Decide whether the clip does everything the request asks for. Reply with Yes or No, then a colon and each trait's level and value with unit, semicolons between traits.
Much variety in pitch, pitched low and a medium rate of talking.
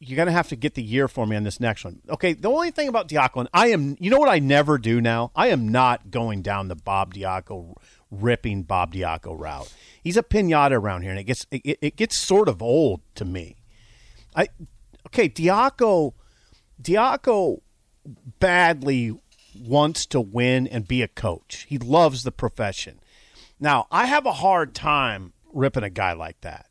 Yes: wide, 6.5 semitones; low, 125 Hz; average, 190 wpm